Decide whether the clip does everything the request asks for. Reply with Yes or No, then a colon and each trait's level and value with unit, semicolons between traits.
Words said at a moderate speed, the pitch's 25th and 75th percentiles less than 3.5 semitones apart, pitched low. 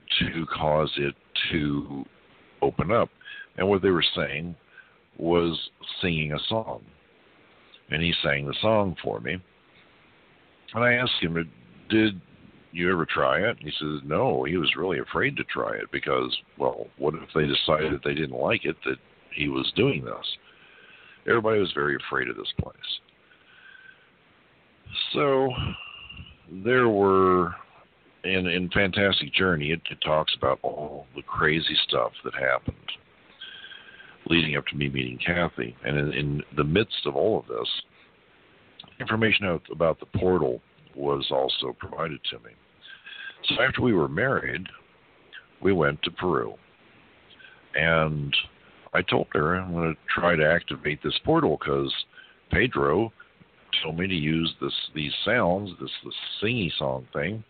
No: average, 145 wpm; average, 4.8 semitones; very low, 85 Hz